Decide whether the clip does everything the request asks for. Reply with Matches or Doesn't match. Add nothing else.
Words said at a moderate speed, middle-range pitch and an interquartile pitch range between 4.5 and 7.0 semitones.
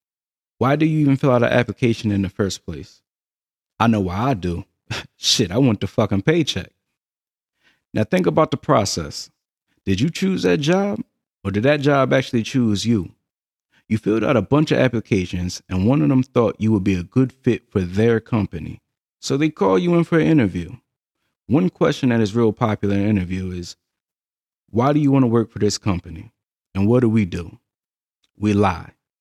Doesn't match